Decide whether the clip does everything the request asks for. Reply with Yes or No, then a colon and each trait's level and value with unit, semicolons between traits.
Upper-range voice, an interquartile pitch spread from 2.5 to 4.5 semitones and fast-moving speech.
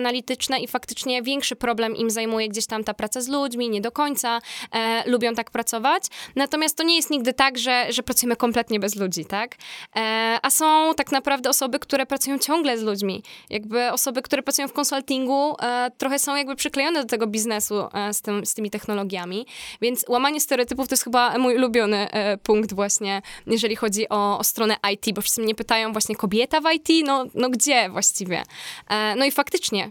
Yes: high, 240 Hz; average, 4.0 semitones; fast, 195 wpm